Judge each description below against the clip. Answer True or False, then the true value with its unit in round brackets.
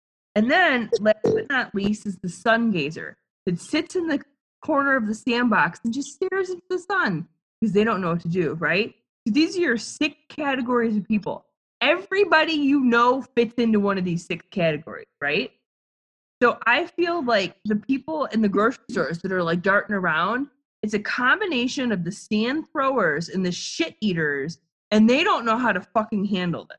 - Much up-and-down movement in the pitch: True (6.3 semitones)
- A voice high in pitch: True (225 Hz)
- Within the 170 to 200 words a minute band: True (190 wpm)